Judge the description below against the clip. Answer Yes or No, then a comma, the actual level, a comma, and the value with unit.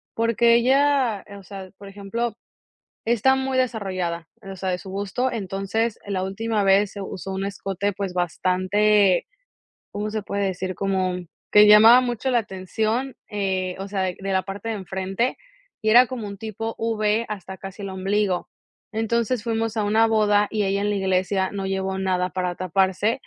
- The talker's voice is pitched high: Yes, high, 200 Hz